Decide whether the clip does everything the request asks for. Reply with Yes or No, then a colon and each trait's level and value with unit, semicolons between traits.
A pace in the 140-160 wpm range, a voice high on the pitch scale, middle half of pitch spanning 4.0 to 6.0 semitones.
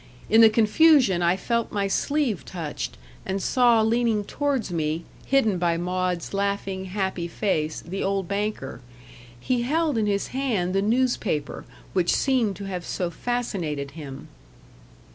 Yes: average, 145 wpm; high, 200 Hz; average, 4.9 semitones